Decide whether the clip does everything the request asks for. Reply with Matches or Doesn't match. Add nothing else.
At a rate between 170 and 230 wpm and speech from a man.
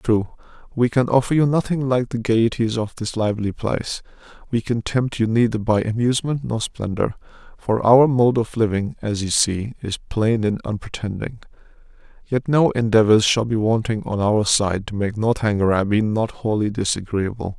Matches